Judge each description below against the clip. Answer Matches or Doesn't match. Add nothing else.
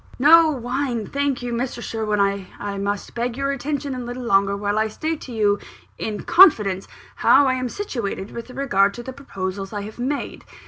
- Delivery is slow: Doesn't match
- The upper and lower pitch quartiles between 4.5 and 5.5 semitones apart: Matches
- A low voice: Doesn't match